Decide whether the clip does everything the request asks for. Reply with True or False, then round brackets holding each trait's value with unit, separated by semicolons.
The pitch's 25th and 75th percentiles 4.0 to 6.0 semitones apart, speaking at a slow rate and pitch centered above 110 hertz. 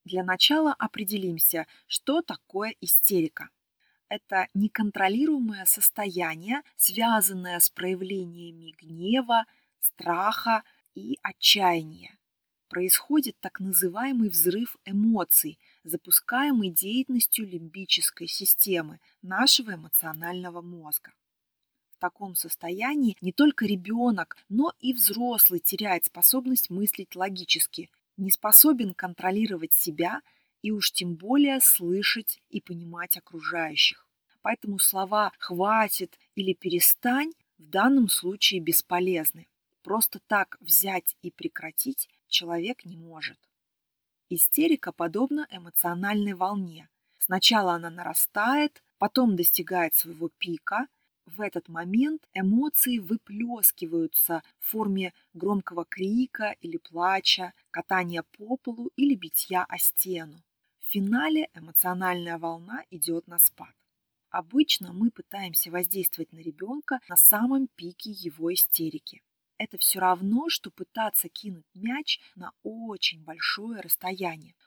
True (4.6 semitones; 105 wpm; 190 Hz)